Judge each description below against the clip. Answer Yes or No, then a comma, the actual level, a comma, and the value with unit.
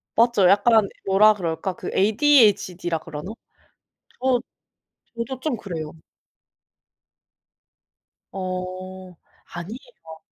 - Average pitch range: Yes, average, 4.2 semitones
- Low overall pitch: No, high, 195 Hz